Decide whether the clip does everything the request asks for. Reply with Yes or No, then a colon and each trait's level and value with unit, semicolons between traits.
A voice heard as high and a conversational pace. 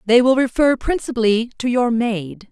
Yes: high, 235 Hz; average, 165 wpm